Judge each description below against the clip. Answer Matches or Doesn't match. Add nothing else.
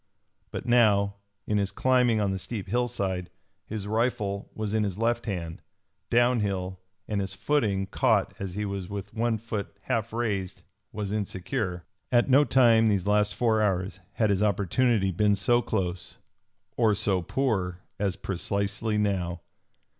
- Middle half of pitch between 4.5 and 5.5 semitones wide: Doesn't match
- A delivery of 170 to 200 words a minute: Doesn't match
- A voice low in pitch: Matches